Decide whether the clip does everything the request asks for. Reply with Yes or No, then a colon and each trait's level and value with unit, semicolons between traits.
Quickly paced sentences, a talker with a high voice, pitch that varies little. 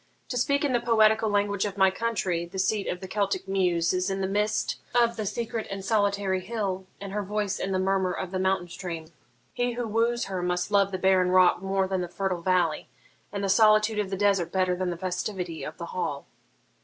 Yes: fast, 220 wpm; high, 195 Hz; narrow, 2.3 semitones